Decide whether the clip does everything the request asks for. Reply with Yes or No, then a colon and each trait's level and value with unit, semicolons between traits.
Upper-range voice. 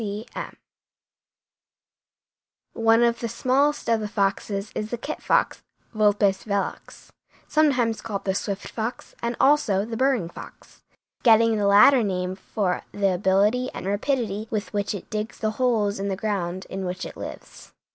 Yes: high, 210 Hz